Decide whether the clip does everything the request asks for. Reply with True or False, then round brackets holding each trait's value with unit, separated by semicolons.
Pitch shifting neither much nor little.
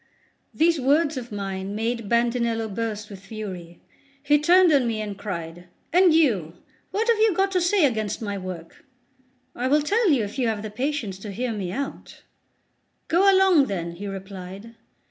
False (7.2 semitones)